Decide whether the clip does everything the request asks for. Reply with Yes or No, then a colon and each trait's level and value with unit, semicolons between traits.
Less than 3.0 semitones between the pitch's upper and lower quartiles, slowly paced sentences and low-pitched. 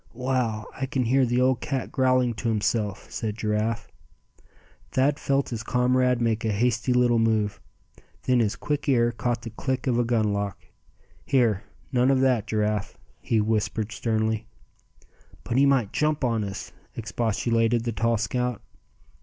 No: narrow, 2.6 semitones; average, 155 wpm; low, 115 Hz